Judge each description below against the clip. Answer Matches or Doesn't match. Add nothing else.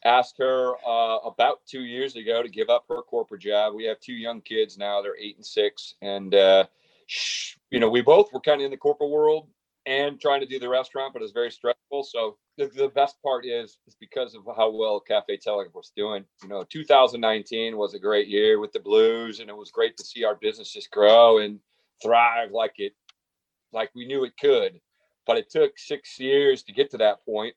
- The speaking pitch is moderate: Matches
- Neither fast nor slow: Doesn't match